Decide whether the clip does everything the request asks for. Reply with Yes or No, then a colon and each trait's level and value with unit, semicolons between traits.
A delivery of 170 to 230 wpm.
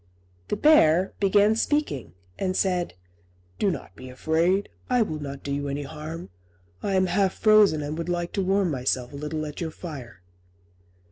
Yes: average, 175 wpm